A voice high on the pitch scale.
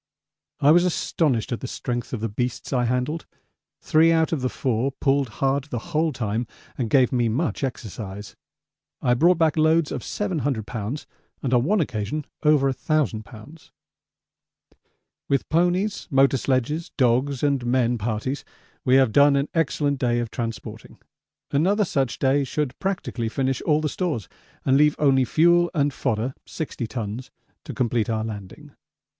No: low, 135 Hz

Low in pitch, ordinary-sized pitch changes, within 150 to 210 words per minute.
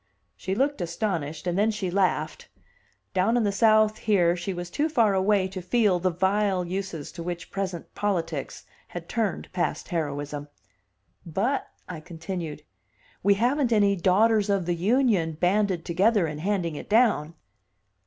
No: high, 190 Hz; average, 3.7 semitones; average, 155 wpm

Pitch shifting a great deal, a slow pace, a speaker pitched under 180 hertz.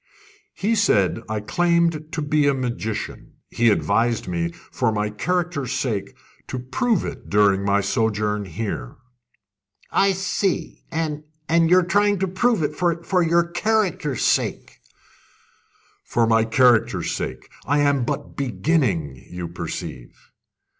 Yes: wide, 8.4 semitones; slow, 130 wpm; low, 135 Hz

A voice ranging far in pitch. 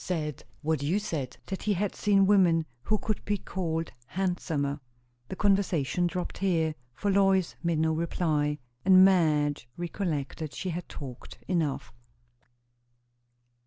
No: average, 4.0 semitones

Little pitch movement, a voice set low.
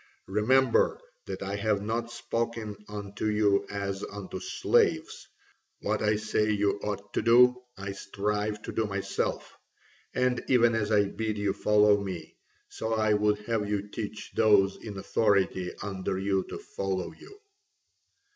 Yes: narrow, 1.9 semitones; low, 105 Hz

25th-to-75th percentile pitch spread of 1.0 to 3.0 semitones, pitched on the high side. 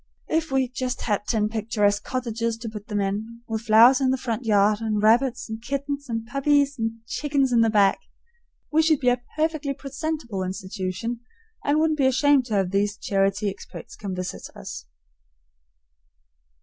No: average, 4.5 semitones; high, 230 Hz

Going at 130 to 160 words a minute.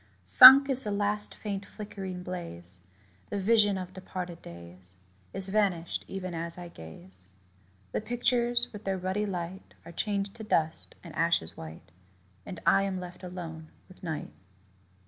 Yes: average, 150 wpm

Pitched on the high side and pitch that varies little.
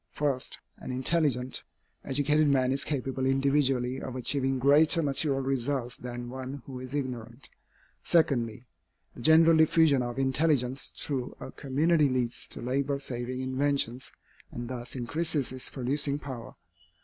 No: low, 135 Hz; narrow, 2.3 semitones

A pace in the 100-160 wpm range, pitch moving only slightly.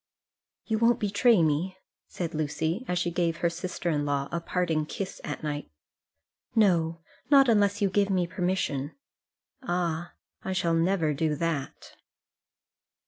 No: average, 140 wpm; average, 3.4 semitones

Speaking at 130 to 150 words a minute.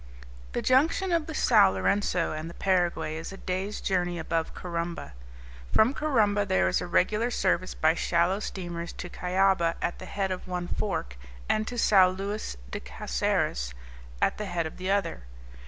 No: average, 170 wpm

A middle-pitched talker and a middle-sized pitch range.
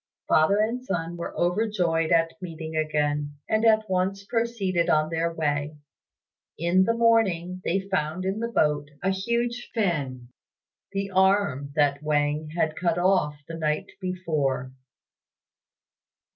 Yes: medium, 170 Hz; average, 4.3 semitones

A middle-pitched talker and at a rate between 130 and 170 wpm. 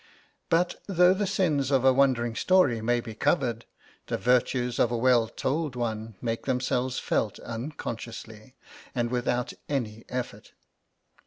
No: low, 125 Hz; average, 140 wpm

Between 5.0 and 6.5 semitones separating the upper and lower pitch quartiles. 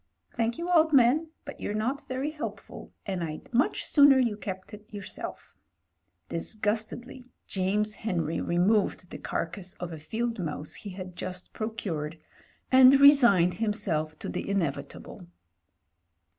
Yes: wide, 5.6 semitones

